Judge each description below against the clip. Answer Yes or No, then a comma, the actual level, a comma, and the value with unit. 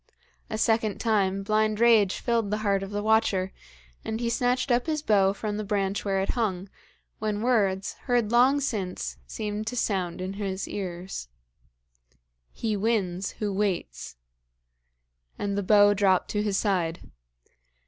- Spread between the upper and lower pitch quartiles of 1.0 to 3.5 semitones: Yes, narrow, 2.4 semitones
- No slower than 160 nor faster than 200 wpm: No, average, 150 wpm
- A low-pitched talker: No, high, 205 Hz